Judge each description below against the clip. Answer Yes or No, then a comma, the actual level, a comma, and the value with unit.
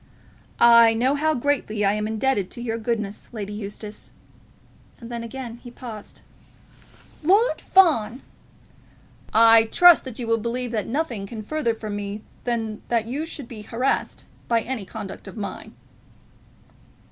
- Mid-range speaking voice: No, high, 230 Hz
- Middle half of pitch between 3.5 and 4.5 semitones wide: No, average, 2.9 semitones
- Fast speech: No, average, 150 wpm